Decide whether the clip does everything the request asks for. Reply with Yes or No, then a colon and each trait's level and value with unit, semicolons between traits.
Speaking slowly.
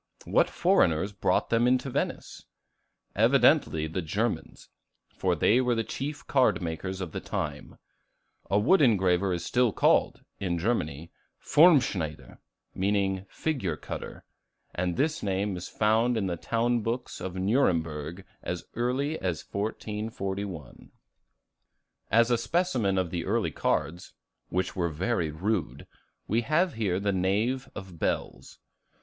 Yes: slow, 130 wpm